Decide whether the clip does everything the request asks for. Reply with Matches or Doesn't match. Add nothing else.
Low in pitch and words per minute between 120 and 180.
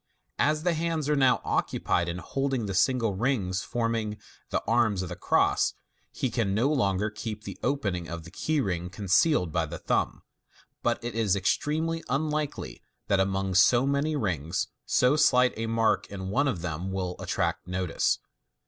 Matches